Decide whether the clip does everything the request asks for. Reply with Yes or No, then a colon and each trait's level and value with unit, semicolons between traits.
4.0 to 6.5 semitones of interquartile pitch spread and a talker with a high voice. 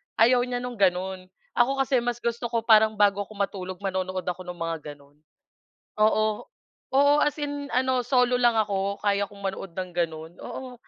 Yes: average, 4.4 semitones; high, 205 Hz